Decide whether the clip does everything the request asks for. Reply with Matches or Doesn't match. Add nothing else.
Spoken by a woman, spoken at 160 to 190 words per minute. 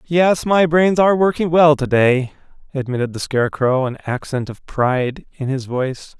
Doesn't match